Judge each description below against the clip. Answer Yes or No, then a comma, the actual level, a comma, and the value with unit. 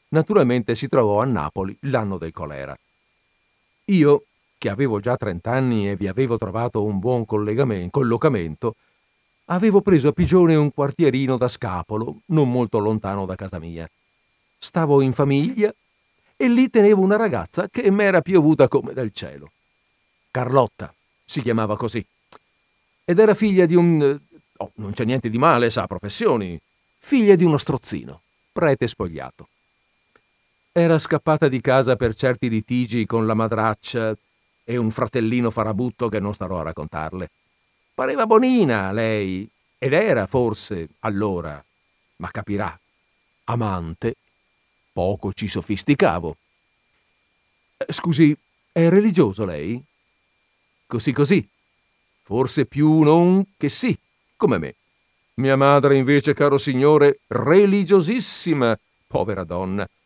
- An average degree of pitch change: No, wide, 6.8 semitones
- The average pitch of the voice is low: Yes, low, 125 Hz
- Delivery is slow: No, average, 125 wpm